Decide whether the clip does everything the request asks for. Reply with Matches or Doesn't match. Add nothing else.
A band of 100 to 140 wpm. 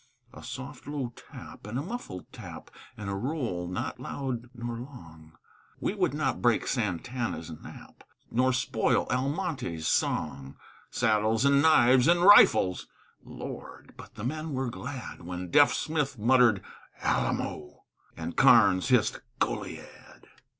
Matches